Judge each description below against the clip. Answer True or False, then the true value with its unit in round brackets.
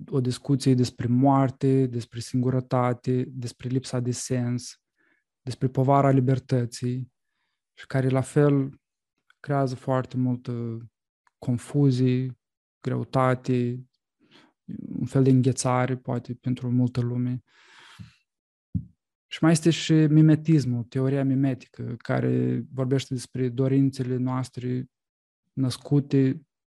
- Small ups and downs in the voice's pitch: True (1.5 semitones)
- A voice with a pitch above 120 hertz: True (130 Hz)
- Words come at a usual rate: False (95 wpm)